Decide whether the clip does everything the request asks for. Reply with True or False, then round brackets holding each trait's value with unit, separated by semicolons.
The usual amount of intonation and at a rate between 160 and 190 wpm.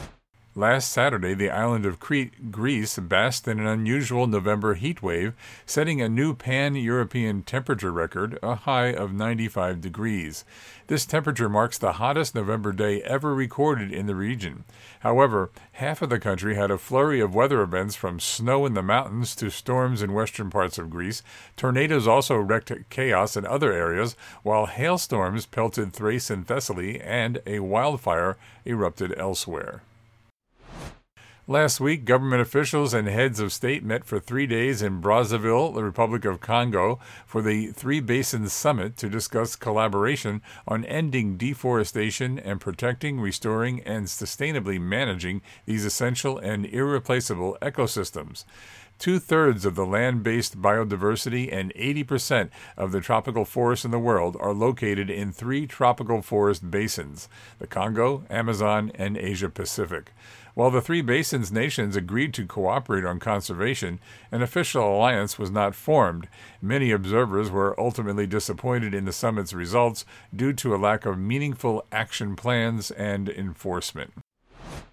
False (3.7 semitones; 145 wpm)